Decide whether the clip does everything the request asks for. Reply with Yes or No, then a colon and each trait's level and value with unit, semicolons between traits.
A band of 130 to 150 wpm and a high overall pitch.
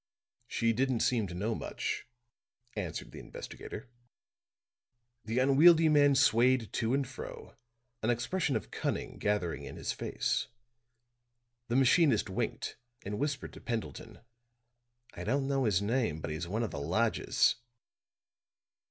No: slow, 135 wpm; low, 120 Hz